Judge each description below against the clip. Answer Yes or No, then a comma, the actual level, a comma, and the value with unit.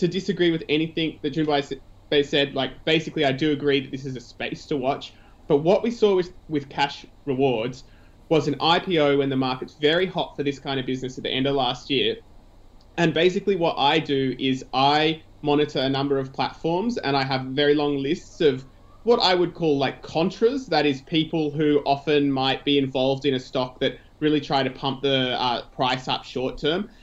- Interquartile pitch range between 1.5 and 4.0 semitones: Yes, average, 3.0 semitones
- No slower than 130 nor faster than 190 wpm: No, fast, 205 wpm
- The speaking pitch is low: No, medium, 145 Hz